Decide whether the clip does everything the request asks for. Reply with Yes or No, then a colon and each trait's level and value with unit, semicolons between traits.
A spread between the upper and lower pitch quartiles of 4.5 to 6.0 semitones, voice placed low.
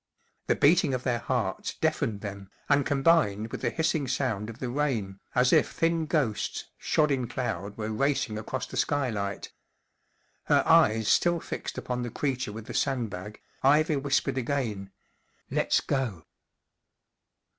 Yes: average, 4.9 semitones; low, 125 Hz